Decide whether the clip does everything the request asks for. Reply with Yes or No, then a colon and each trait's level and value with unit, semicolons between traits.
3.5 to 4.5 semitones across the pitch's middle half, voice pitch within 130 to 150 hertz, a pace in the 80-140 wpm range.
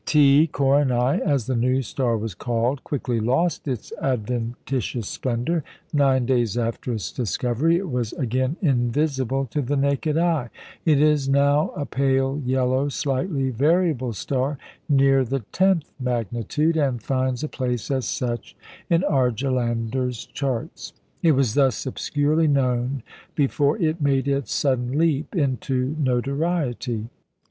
No: average, 2.8 semitones; low, 135 Hz; slow, 135 wpm